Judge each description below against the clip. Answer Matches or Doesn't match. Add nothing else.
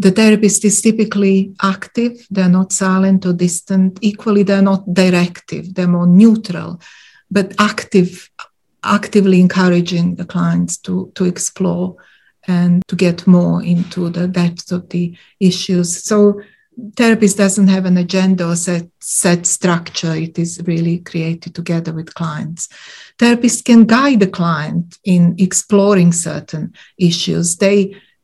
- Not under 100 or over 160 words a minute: Matches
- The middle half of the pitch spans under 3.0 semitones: Matches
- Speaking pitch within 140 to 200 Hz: Matches